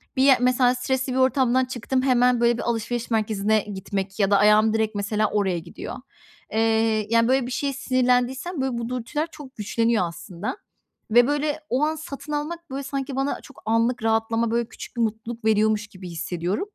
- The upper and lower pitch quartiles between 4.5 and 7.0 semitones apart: No, average, 3.4 semitones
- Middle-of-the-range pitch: No, high, 235 Hz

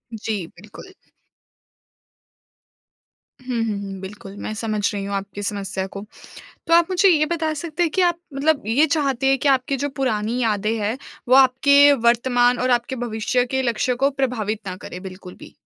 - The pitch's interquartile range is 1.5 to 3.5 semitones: No, average, 4.8 semitones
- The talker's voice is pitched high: Yes, high, 245 Hz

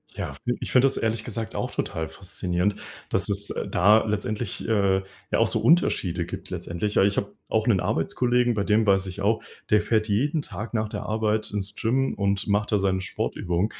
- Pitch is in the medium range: No, low, 105 Hz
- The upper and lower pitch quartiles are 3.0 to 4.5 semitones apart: No, narrow, 2.4 semitones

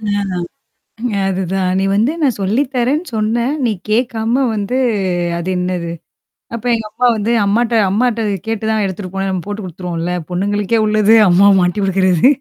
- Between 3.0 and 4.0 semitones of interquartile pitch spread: Yes, average, 3.7 semitones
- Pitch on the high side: Yes, high, 210 Hz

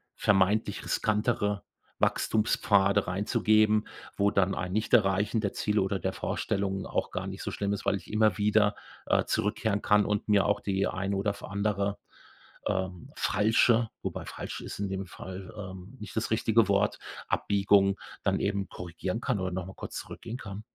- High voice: No, low, 100 Hz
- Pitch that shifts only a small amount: Yes, narrow, 1.6 semitones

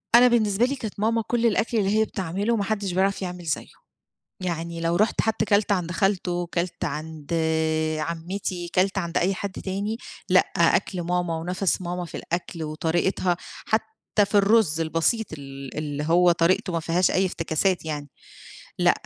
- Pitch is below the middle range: No, medium, 180 Hz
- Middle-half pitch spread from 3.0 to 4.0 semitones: Yes, average, 3.3 semitones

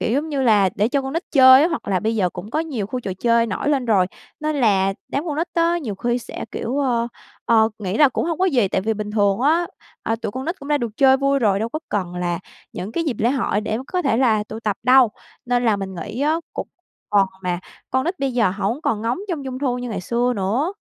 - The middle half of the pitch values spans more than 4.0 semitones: Yes, average, 4.9 semitones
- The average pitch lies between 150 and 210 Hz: No, high, 240 Hz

